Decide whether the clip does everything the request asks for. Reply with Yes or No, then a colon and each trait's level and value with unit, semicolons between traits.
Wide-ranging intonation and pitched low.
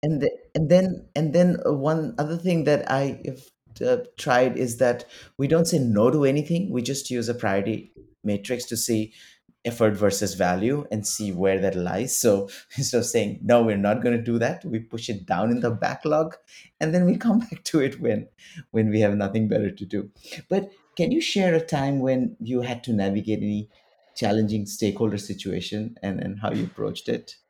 Yes: wide, 6.3 semitones; low, 120 Hz